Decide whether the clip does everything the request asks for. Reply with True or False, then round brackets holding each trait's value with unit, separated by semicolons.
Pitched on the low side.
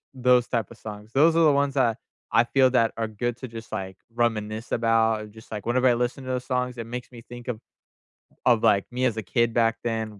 True (120 Hz)